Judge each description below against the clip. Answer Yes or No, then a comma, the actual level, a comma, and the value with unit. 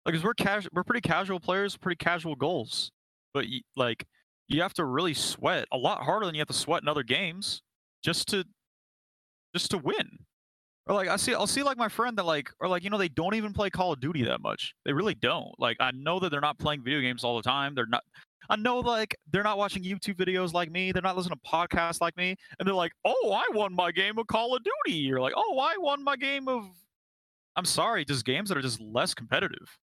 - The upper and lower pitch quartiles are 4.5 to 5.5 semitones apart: Yes, average, 5.0 semitones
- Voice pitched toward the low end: No, medium, 185 Hz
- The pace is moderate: No, fast, 245 wpm